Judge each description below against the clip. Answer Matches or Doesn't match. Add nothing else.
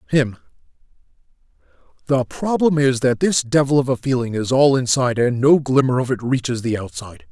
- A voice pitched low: Matches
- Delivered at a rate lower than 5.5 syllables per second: Doesn't match